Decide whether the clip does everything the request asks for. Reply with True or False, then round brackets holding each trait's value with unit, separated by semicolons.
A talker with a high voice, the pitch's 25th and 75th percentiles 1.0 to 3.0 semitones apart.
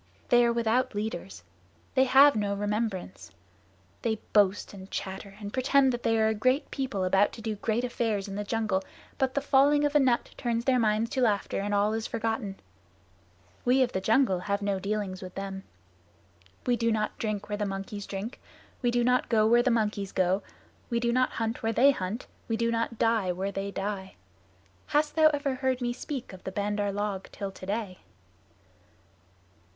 False (220 Hz; 3.4 semitones)